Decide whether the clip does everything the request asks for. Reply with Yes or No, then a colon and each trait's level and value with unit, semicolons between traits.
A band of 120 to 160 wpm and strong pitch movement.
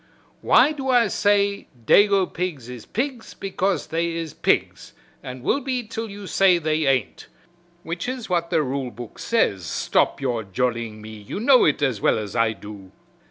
No: average, 175 wpm; wide, 9.0 semitones